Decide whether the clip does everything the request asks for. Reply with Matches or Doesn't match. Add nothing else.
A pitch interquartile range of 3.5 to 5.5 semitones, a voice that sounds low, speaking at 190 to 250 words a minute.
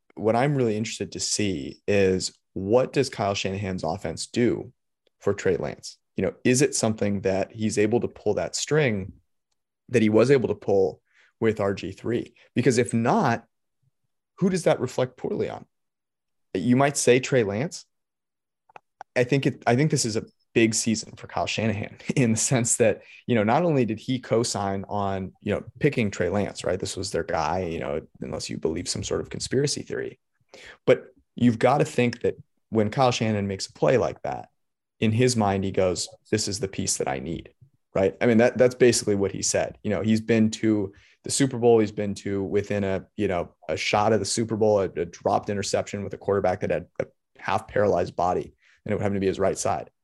Matches